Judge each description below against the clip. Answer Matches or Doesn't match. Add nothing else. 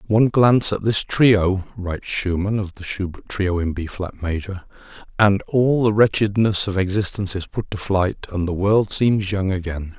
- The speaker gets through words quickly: Doesn't match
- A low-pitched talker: Matches